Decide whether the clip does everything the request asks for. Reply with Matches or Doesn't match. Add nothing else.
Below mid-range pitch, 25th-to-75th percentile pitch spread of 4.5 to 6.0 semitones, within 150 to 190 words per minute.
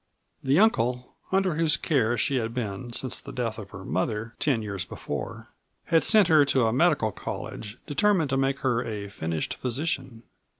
Matches